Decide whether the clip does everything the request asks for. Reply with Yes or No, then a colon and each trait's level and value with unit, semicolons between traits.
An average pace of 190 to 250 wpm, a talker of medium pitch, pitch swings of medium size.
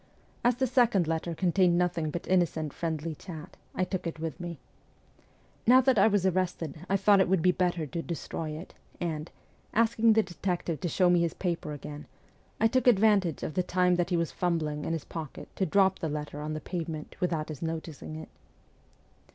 Yes: average, 200 wpm; medium, 175 Hz; average, 3.2 semitones